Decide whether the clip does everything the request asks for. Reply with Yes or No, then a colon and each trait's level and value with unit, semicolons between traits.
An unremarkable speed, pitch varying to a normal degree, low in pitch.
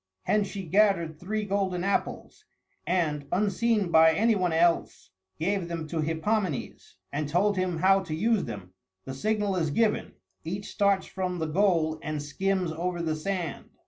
No: average, 160 wpm; average, 3.8 semitones; medium, 180 Hz